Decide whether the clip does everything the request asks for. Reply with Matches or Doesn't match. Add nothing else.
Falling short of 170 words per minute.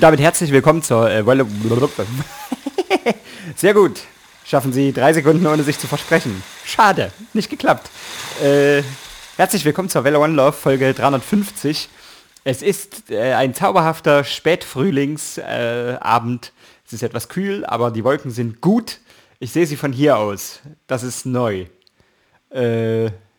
Matches